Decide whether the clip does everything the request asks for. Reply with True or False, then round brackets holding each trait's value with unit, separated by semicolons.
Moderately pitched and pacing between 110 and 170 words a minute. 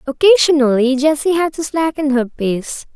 False (290 Hz; 140 wpm)